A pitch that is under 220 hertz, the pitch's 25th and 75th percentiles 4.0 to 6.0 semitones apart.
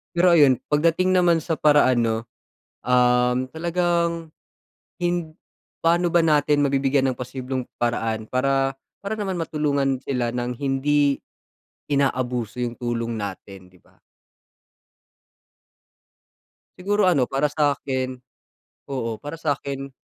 Yes: low, 135 Hz; average, 4.6 semitones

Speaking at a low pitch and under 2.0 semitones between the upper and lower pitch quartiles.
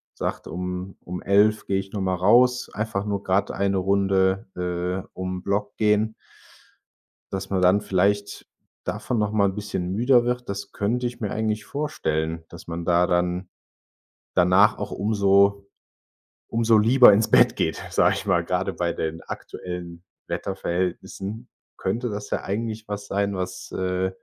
No: low, 100 Hz; narrow, 2.6 semitones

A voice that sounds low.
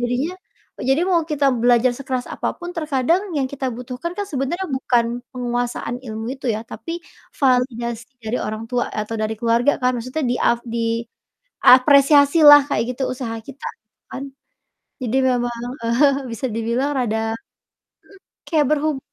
No: very high, 255 Hz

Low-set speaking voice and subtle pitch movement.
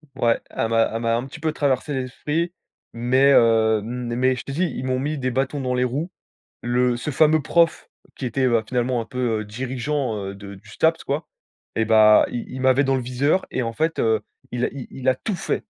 No: low, 125 Hz; average, 3.1 semitones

